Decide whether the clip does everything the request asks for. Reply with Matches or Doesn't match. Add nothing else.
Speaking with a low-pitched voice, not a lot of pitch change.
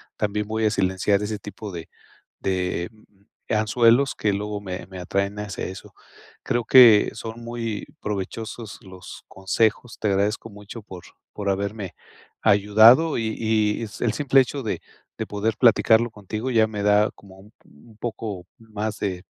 Matches